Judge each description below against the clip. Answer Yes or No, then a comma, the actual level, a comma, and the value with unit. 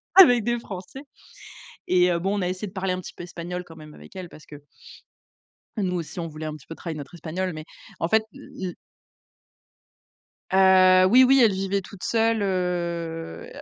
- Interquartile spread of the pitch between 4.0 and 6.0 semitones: No, average, 2.7 semitones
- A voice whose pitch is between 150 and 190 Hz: Yes, medium, 185 Hz